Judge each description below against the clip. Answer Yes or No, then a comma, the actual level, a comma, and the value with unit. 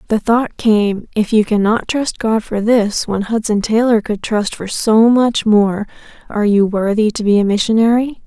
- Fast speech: No, average, 180 wpm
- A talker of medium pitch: No, high, 215 Hz